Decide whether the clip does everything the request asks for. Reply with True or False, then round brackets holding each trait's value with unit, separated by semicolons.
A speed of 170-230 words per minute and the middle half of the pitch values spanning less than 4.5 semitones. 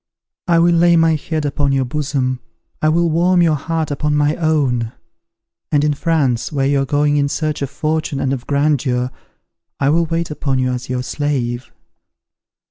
True (180 wpm; 2.9 semitones)